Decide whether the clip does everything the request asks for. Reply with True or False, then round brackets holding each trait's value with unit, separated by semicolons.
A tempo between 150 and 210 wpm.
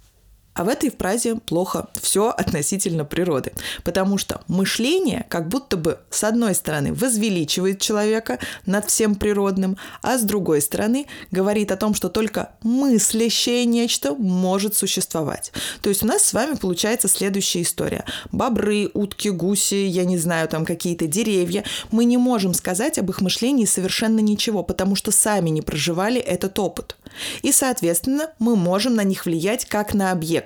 True (155 wpm)